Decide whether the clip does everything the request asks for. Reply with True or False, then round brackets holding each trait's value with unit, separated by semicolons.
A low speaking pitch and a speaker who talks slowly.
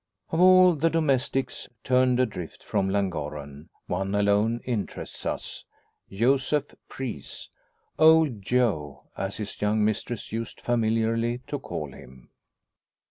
True (115 Hz; 115 wpm)